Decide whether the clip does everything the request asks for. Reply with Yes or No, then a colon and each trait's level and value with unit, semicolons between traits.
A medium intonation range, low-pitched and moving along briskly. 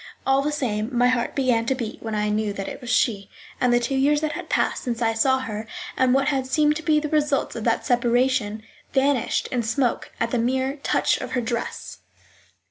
No: average, 3.0 semitones; very high, 250 Hz; fast, 220 wpm